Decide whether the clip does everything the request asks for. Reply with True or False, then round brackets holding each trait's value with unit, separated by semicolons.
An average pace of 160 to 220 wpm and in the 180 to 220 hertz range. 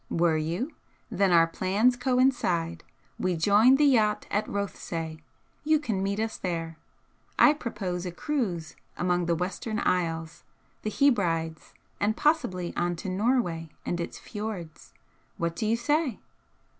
False (140 wpm; 190 Hz)